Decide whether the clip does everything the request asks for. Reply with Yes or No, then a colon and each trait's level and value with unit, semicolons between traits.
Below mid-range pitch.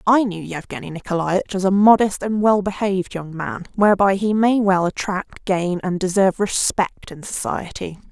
No: high, 190 Hz